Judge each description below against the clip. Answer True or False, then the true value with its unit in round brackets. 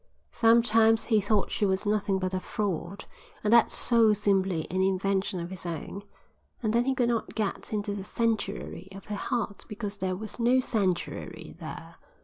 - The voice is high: True (205 Hz)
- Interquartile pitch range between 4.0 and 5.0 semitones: False (2.9 semitones)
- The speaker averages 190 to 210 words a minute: False (175 wpm)